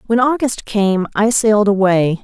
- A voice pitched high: Yes, high, 210 Hz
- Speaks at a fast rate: No, average, 160 wpm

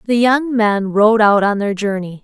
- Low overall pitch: No, high, 215 Hz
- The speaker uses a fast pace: Yes, fast, 215 wpm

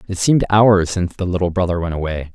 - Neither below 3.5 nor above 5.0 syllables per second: No, 6.5 syllables/s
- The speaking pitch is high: No, very low, 90 Hz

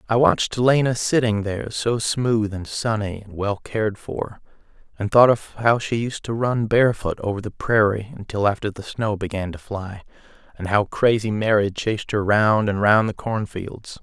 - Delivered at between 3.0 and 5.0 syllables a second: Yes, 4.8 syllables/s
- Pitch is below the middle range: Yes, low, 105 Hz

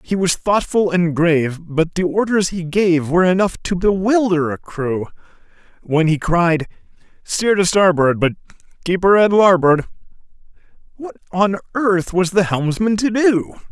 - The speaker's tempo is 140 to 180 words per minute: Yes, average, 150 wpm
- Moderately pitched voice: Yes, medium, 180 Hz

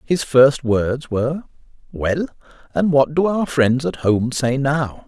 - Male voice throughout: Yes, male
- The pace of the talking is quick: No, average, 165 wpm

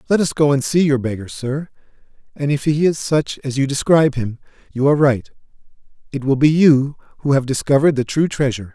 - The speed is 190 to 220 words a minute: Yes, average, 200 wpm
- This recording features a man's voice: Yes, male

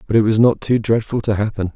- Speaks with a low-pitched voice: Yes, low, 110 Hz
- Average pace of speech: No, fast, 275 wpm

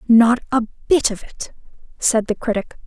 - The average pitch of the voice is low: No, high, 230 Hz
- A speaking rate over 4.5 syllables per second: No, 4.3 syllables/s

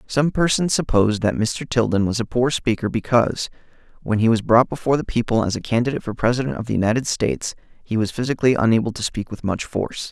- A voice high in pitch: No, low, 120 Hz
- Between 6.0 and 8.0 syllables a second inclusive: Yes, 6.5 syllables/s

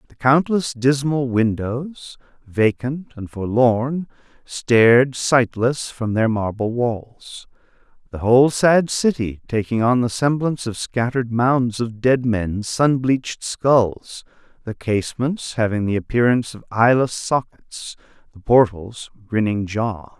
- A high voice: No, low, 120 Hz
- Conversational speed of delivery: No, slow, 120 wpm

